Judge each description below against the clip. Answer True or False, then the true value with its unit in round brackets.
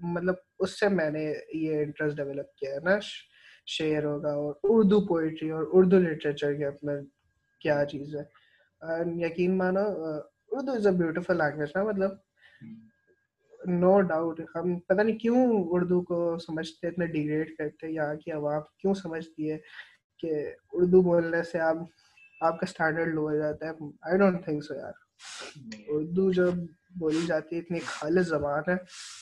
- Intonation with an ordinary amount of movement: True (3.4 semitones)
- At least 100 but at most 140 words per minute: False (155 wpm)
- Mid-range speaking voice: True (165 Hz)